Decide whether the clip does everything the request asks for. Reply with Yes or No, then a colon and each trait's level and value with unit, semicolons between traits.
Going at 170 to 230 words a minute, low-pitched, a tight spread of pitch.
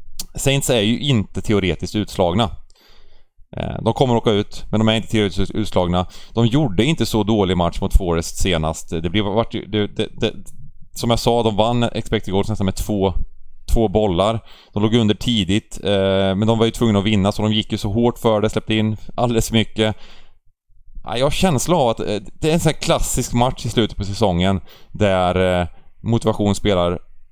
No: average, 190 wpm; low, 105 Hz; average, 3.0 semitones